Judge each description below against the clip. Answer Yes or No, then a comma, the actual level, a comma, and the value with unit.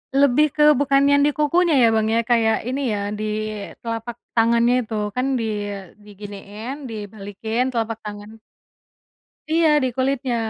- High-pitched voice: Yes, high, 230 Hz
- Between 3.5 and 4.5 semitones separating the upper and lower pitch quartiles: Yes, average, 3.9 semitones